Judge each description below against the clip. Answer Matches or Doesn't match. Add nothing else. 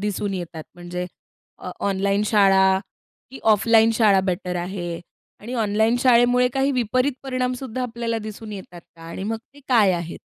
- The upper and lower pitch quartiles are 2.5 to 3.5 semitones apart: Doesn't match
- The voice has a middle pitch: Doesn't match